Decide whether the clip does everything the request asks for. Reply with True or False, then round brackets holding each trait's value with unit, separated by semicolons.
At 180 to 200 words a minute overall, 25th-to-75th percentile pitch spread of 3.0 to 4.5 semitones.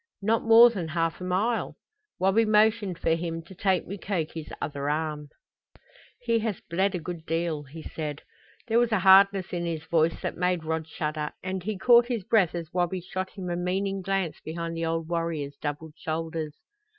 True (185 wpm; 3.4 semitones)